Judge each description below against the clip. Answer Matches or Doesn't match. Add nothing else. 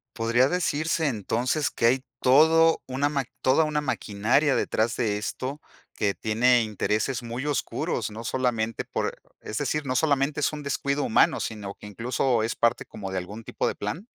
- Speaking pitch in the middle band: Doesn't match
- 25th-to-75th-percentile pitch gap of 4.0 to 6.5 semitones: Matches